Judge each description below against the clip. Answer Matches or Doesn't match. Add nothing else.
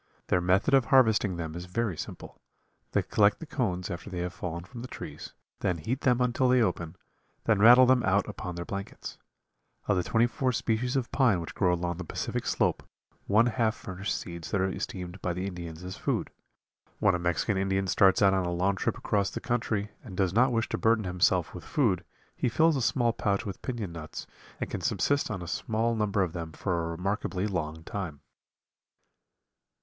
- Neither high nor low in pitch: Doesn't match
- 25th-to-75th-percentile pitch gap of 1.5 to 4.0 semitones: Doesn't match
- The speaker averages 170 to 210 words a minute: Matches